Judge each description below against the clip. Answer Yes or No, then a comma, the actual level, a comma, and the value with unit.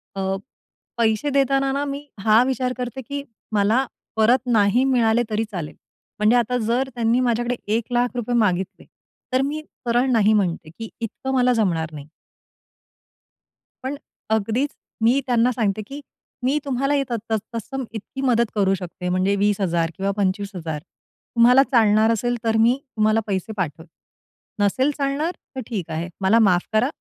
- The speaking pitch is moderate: No, high, 230 Hz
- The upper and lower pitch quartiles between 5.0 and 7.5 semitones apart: No, average, 4.0 semitones